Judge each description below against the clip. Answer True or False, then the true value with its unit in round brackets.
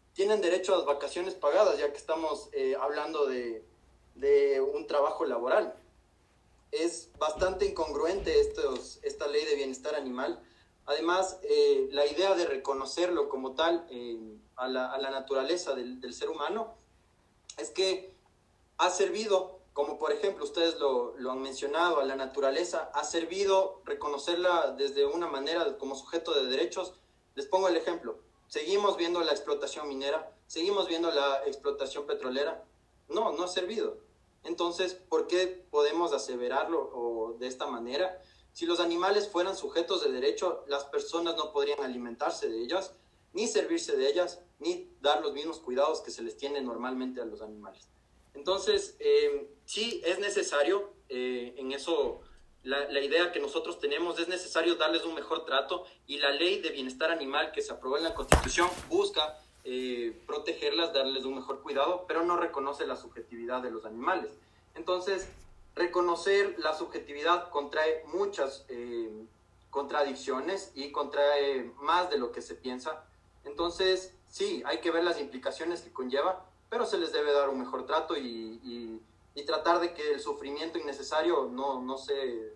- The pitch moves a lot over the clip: True (6.5 semitones)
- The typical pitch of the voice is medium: True (170 Hz)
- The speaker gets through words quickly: False (160 wpm)